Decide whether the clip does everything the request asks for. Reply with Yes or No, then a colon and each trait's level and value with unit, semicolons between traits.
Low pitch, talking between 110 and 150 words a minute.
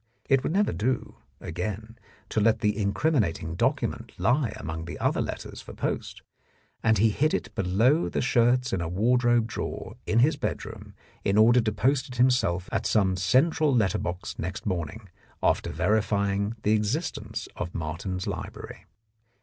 No: low, 110 Hz; average, 160 wpm